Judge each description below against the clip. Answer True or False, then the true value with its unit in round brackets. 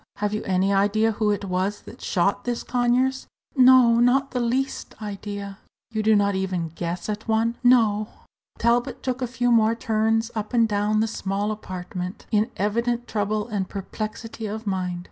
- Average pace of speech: True (175 wpm)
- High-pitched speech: True (215 Hz)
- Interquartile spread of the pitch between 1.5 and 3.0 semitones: True (2.7 semitones)